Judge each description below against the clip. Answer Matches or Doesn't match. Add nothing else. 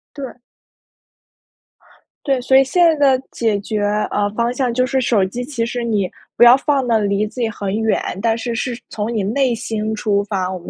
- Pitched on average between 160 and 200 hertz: Doesn't match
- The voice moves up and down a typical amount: Matches